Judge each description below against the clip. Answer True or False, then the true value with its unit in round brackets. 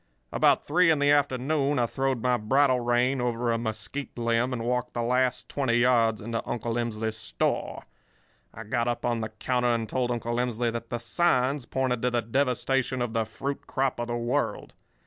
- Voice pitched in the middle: False (120 Hz)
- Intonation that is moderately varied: False (2.0 semitones)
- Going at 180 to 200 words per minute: True (190 wpm)